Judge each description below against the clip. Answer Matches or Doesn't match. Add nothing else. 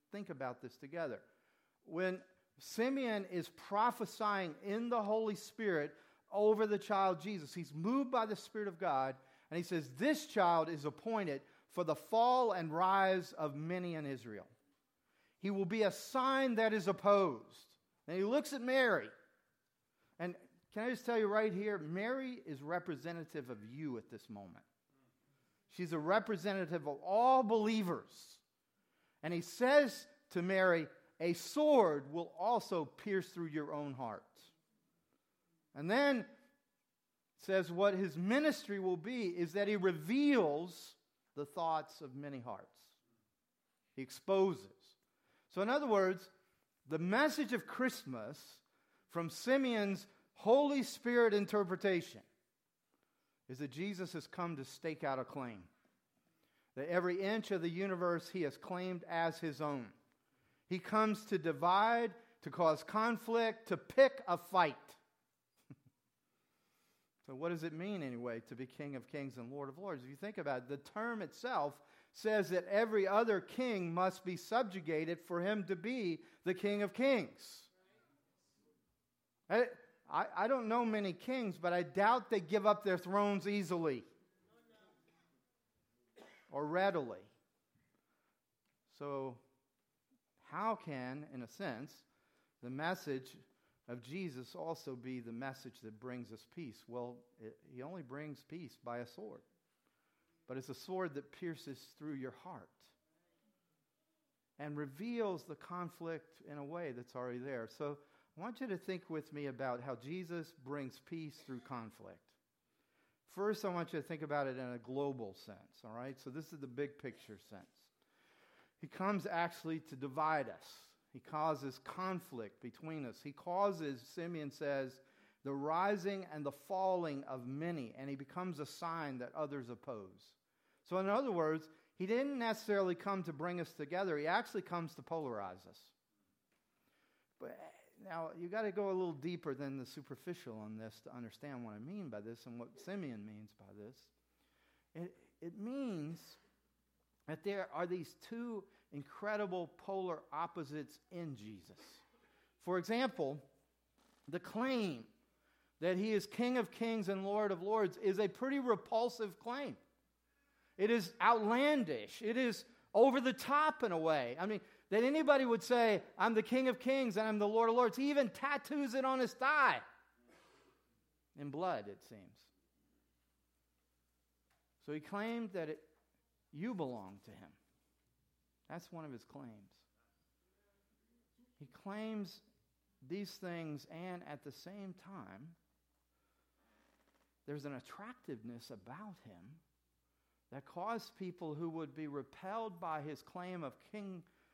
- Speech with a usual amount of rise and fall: Doesn't match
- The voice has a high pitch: Doesn't match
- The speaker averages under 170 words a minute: Matches